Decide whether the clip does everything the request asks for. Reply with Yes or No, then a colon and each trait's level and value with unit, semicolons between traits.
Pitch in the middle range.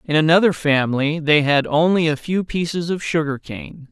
Yes: medium, 155 Hz